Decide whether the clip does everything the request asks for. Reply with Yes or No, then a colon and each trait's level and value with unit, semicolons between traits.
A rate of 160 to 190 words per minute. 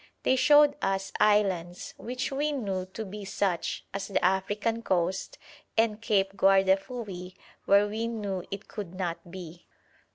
No: average, 140 wpm